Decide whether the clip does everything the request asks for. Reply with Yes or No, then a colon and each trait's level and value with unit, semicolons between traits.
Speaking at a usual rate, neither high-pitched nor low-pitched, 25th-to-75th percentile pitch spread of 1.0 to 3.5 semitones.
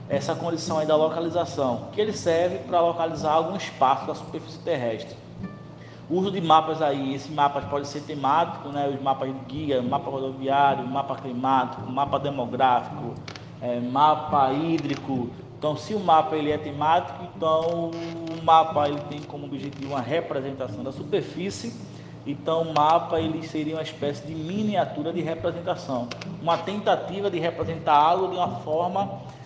Yes: average, 155 wpm; medium, 155 Hz; average, 3.0 semitones